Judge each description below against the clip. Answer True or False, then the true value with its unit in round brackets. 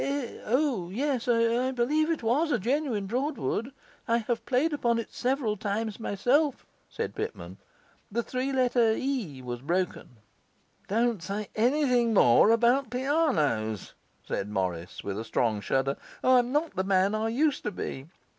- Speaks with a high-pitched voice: True (235 Hz)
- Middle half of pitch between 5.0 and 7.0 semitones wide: True (5.6 semitones)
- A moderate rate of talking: True (155 wpm)